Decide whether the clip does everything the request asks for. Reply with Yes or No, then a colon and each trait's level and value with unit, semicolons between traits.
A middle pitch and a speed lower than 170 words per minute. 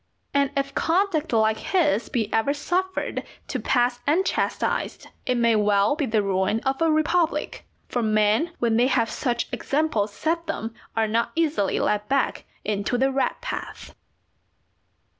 No: very high, 250 Hz; average, 150 wpm